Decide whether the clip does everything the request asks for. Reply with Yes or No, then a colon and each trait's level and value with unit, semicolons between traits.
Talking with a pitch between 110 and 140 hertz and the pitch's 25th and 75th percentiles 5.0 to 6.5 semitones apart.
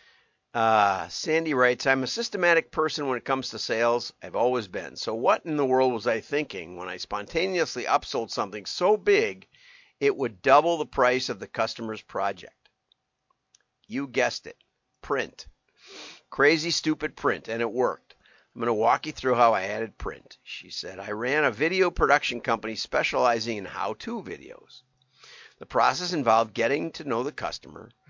Yes: low, 135 Hz; wide, 5.4 semitones